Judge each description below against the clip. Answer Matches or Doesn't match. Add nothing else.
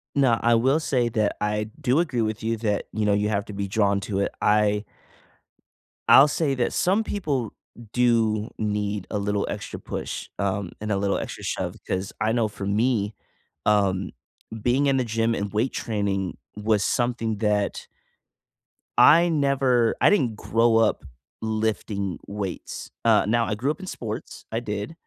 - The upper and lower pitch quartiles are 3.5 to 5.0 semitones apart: Doesn't match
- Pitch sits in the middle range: Doesn't match